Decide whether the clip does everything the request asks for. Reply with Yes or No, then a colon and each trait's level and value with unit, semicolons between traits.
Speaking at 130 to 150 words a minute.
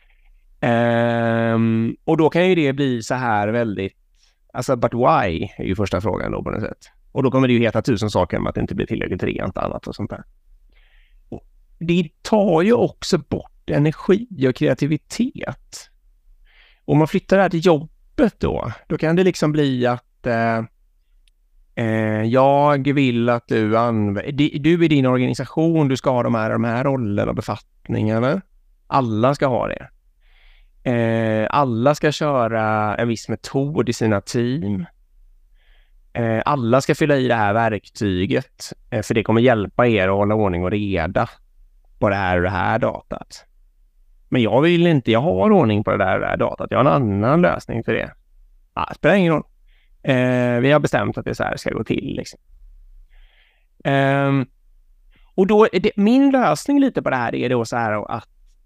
No: average, 180 wpm